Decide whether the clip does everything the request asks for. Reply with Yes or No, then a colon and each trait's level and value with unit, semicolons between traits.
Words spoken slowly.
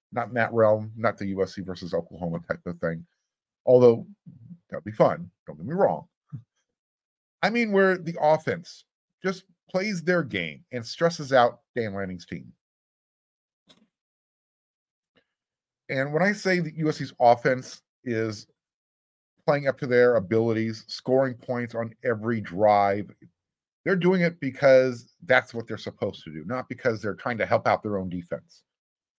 No: average, 150 wpm